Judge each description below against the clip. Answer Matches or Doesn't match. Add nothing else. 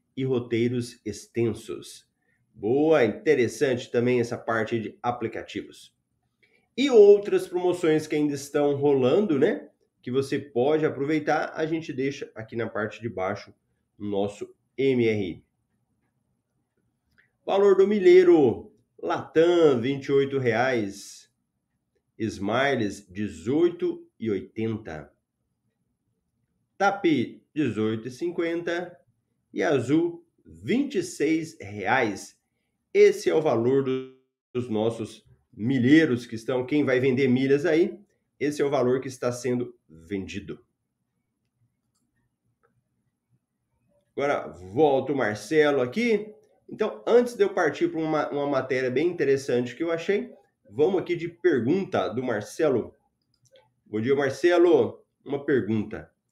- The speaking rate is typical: Doesn't match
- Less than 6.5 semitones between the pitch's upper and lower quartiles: Doesn't match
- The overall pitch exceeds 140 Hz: Doesn't match